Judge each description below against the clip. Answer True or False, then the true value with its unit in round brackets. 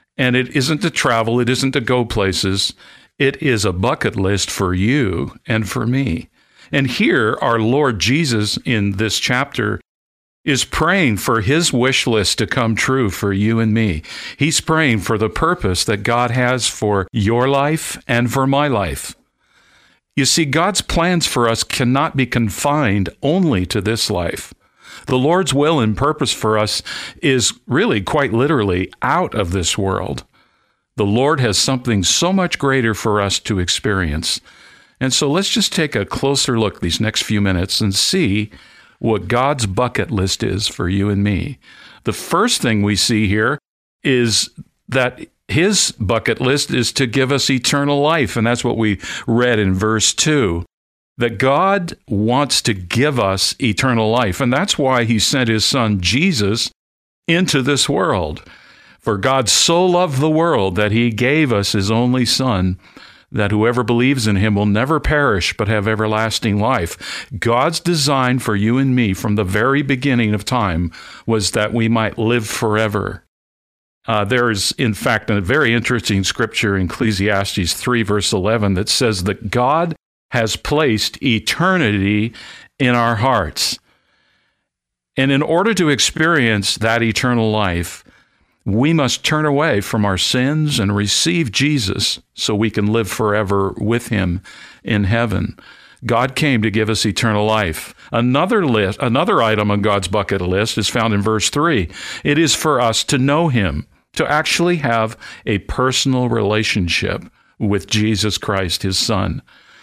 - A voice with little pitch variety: False (4.3 semitones)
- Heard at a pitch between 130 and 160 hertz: False (115 Hz)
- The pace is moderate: True (160 wpm)